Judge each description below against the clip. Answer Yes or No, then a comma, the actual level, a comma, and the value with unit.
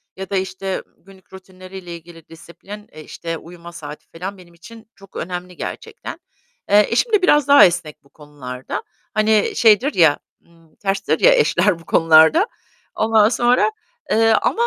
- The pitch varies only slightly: No, average, 4.5 semitones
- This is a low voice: No, medium, 185 Hz